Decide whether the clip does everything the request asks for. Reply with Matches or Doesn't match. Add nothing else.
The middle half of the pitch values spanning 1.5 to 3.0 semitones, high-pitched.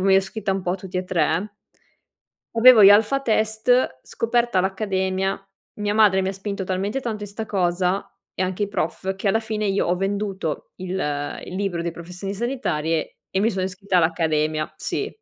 Matches